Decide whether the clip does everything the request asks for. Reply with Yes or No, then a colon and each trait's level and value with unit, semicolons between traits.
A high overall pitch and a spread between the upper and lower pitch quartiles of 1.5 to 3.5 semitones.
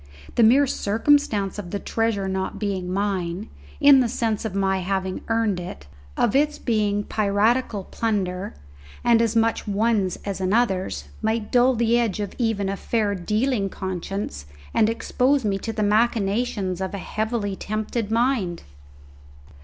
Yes: high, 210 Hz; average, 3.0 semitones